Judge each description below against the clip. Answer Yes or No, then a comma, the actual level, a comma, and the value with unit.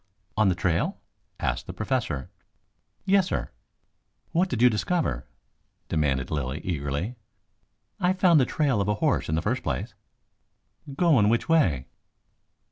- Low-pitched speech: Yes, low, 105 Hz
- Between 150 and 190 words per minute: No, slow, 135 wpm